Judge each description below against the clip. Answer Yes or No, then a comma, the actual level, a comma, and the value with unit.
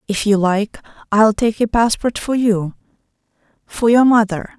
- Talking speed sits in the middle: Yes, average, 155 wpm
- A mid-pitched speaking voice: No, high, 215 Hz